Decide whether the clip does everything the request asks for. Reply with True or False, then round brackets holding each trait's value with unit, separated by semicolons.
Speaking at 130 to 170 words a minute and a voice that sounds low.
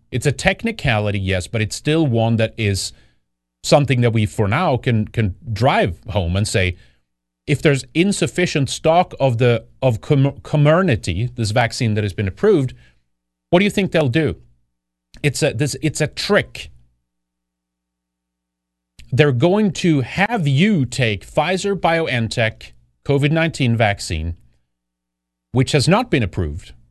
True (140 wpm; 115 Hz)